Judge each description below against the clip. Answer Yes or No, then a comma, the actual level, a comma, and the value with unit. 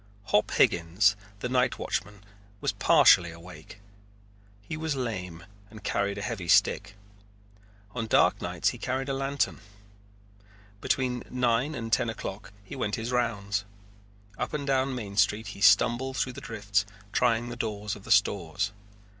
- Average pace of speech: Yes, average, 150 wpm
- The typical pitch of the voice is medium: No, low, 110 Hz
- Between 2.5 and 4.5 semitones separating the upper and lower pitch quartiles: Yes, average, 3.8 semitones